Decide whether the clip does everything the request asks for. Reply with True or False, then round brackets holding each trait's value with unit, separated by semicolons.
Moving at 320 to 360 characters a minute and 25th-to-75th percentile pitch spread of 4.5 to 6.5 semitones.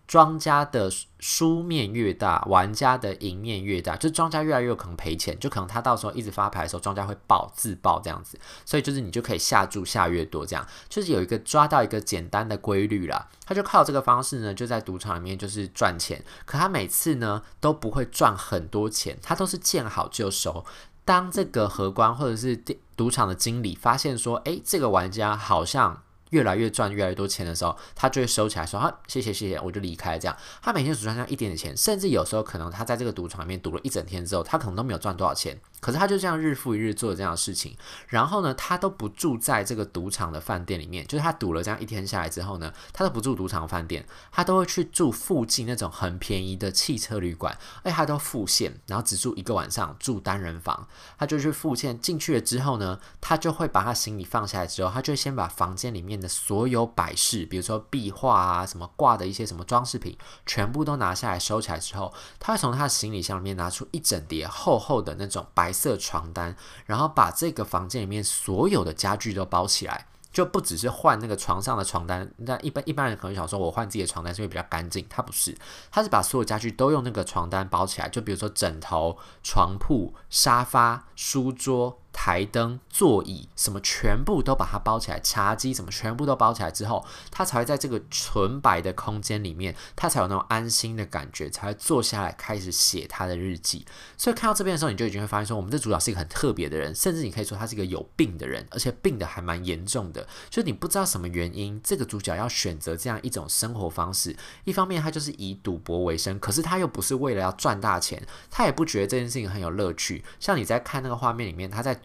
True (355 characters per minute; 5.4 semitones)